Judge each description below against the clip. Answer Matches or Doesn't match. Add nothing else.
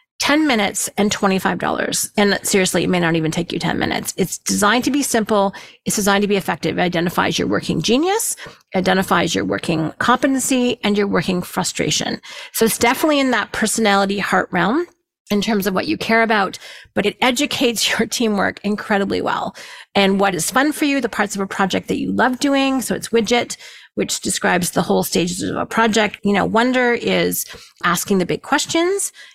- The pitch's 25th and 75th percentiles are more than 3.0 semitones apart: Matches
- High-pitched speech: Matches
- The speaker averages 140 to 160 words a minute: Doesn't match